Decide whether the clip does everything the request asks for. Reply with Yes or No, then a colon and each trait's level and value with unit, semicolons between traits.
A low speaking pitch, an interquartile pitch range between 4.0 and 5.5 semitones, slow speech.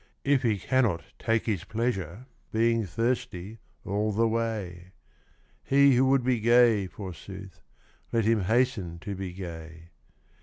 Yes: low, 110 Hz; average, 4.3 semitones; slow, 130 wpm